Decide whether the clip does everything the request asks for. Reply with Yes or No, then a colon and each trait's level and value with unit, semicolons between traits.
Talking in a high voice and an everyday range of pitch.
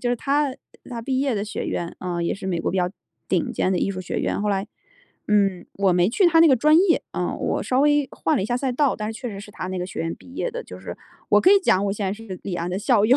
No: high, 210 Hz; wide, 6.2 semitones